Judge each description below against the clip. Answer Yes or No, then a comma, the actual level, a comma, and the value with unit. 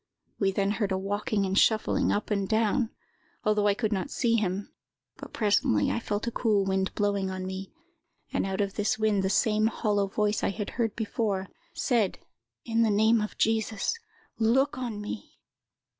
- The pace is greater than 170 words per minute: Yes, average, 180 wpm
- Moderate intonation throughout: No, narrow, 2.1 semitones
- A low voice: No, high, 210 Hz